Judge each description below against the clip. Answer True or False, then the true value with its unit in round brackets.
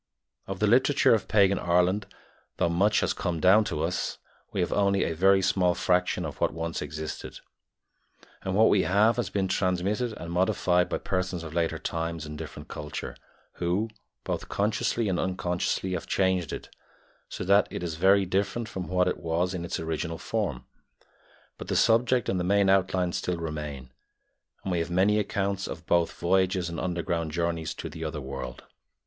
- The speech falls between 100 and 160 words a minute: False (180 wpm)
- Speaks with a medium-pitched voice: False (90 Hz)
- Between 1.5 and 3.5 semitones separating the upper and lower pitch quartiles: True (2.8 semitones)